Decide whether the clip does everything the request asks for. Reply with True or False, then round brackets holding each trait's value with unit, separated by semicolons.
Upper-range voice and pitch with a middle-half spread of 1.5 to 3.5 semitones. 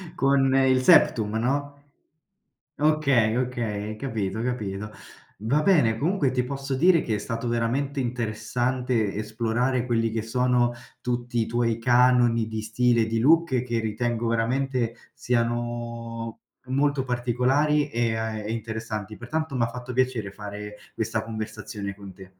False (120 Hz; 2.5 semitones)